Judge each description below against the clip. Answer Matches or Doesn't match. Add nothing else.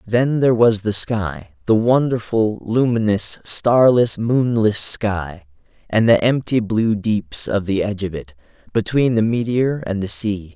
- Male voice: Matches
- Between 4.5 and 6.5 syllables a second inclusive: Doesn't match